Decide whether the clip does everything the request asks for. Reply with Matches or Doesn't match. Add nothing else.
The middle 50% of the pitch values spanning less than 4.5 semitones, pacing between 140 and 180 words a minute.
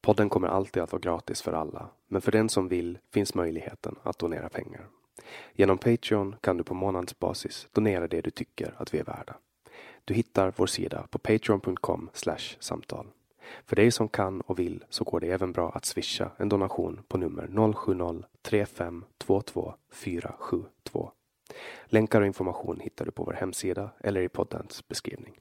Matches